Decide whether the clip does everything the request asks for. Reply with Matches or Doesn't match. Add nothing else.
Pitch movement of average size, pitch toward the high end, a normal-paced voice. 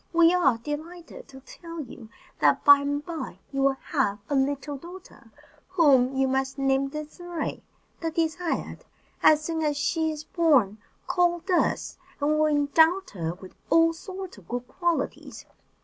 Matches